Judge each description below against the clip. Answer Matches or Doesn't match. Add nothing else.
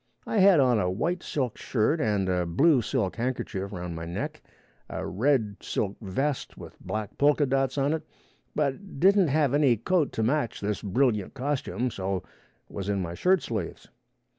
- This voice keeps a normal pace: Matches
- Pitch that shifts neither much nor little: Doesn't match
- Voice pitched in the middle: Doesn't match